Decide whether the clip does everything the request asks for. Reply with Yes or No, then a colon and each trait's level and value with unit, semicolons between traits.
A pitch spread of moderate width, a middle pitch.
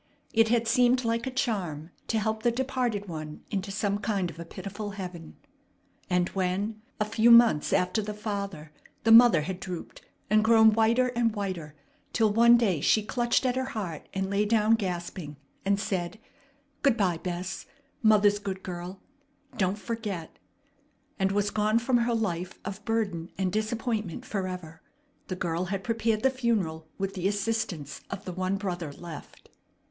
No: average, 3.8 semitones; high, 205 Hz